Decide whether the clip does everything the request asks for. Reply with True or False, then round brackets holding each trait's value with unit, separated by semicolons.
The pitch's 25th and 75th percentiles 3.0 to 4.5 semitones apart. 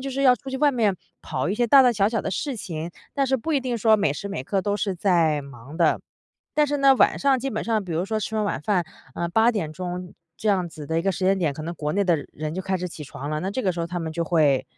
False (5.5 semitones)